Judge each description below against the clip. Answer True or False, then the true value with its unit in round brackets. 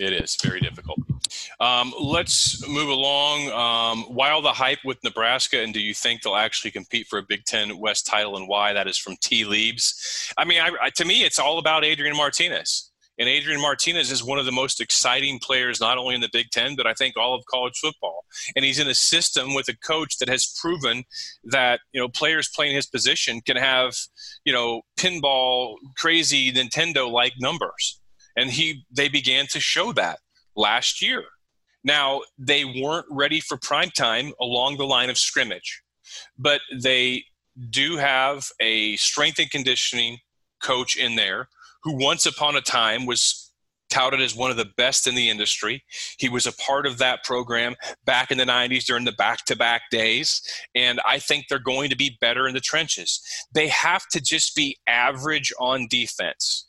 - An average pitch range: True (3.2 semitones)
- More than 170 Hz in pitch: False (135 Hz)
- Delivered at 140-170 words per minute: False (185 wpm)